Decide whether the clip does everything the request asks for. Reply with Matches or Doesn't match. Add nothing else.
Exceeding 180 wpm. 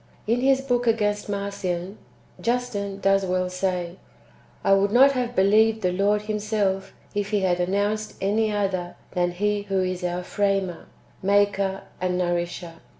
Doesn't match